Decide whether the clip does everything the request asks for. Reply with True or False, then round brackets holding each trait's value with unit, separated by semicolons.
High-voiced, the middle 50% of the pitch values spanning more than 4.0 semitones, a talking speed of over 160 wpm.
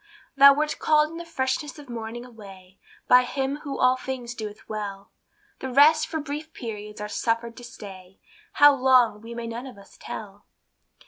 True (245 Hz; 4.7 semitones; 180 wpm)